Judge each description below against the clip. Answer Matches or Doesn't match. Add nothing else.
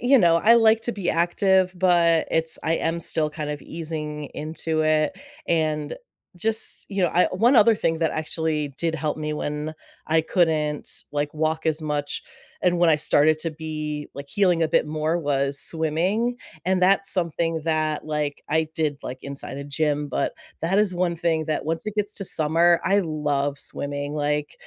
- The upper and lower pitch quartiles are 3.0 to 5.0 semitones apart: Doesn't match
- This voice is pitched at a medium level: Matches